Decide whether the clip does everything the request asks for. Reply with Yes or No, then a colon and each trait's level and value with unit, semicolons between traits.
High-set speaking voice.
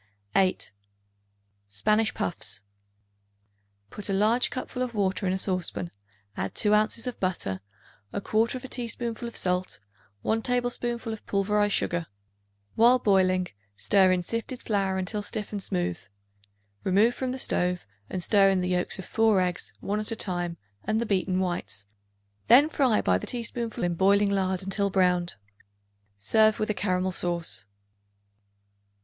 Yes: high, 200 Hz